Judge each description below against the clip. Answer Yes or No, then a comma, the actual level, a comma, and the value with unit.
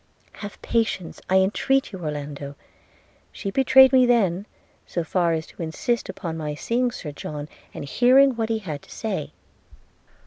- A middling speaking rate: Yes, average, 165 wpm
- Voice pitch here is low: No, high, 190 Hz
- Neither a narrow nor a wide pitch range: No, wide, 7.0 semitones